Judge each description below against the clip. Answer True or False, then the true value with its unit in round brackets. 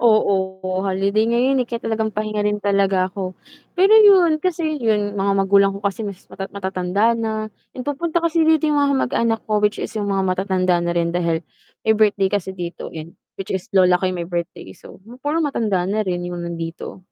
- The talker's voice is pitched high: True (200 Hz)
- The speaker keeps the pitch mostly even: False (3.8 semitones)